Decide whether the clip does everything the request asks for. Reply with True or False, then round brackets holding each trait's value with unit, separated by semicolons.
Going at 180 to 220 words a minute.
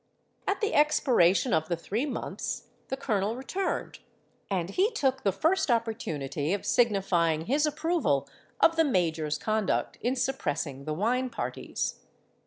False (140 wpm)